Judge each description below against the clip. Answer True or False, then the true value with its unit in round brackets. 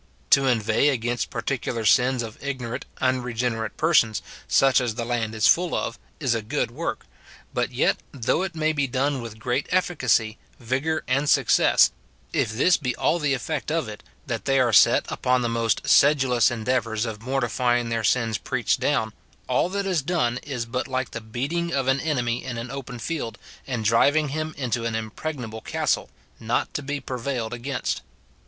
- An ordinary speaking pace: True (180 wpm)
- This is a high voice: False (125 Hz)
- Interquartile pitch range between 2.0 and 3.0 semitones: False (3.4 semitones)